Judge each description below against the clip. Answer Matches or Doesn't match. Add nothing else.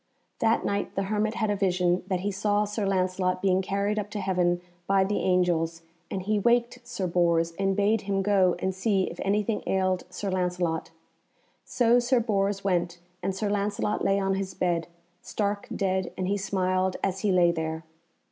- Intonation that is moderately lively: Doesn't match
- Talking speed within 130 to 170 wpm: Doesn't match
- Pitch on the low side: Doesn't match